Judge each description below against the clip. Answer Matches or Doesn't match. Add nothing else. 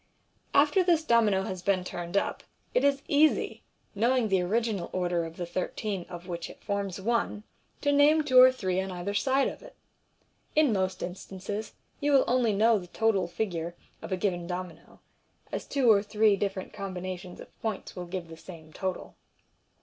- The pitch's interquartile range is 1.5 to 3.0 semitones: Doesn't match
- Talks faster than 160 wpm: Matches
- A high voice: Matches